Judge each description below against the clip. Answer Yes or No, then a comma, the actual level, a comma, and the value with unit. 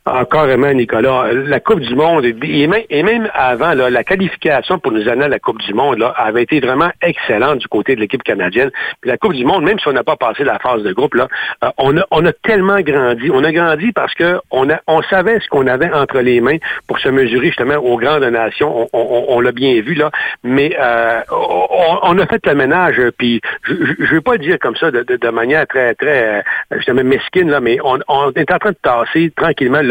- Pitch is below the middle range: No, medium, 150 Hz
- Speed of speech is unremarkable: No, fast, 245 wpm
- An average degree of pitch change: No, wide, 7.2 semitones